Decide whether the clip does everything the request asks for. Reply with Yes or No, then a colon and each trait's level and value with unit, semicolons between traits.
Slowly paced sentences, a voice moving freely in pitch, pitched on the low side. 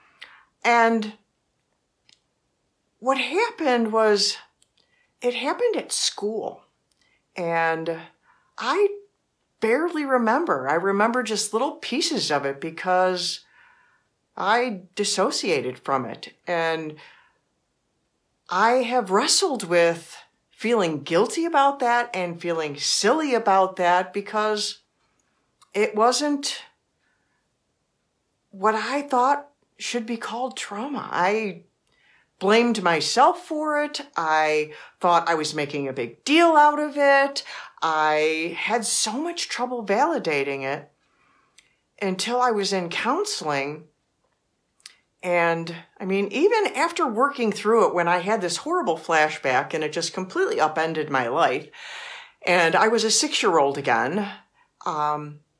No: slow, 115 wpm; wide, 8.5 semitones; high, 215 Hz